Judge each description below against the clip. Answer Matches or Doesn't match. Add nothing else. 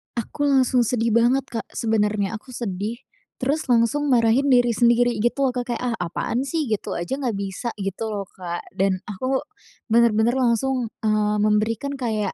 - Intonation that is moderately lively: Matches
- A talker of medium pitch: Doesn't match